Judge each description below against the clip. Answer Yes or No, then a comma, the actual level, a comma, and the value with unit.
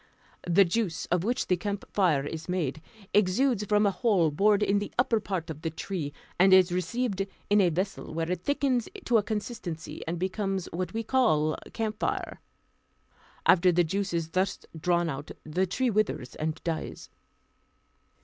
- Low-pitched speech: No, medium, 185 Hz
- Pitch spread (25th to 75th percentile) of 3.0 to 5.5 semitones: Yes, average, 3.9 semitones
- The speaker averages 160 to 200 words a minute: Yes, average, 165 wpm